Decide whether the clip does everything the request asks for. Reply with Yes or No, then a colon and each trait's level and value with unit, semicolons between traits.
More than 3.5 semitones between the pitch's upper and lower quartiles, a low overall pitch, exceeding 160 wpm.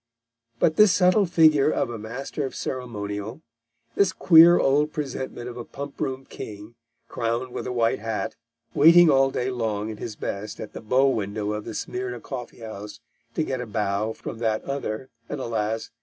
Yes: average, 4.3 semitones; low, 125 Hz; average, 180 wpm